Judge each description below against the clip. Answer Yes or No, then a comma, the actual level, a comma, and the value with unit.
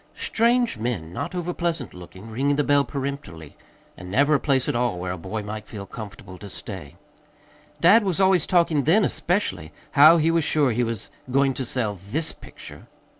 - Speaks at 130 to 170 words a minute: No, average, 180 wpm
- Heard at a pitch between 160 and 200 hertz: No, low, 135 Hz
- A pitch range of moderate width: No, wide, 7.8 semitones